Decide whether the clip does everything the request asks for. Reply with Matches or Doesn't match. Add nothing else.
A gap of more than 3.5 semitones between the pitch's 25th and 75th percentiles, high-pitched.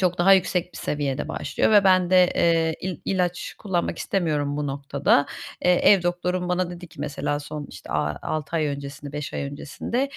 Doesn't match